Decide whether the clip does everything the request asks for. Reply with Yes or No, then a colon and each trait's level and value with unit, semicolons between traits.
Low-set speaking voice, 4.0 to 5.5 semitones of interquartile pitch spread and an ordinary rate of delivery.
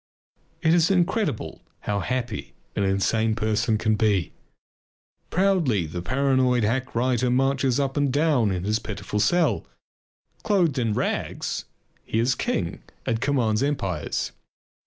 No: low, 125 Hz; average, 4.7 semitones; slow, 130 wpm